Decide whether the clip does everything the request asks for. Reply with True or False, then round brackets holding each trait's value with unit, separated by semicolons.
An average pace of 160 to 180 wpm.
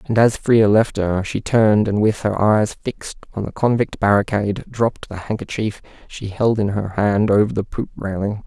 False (200 wpm)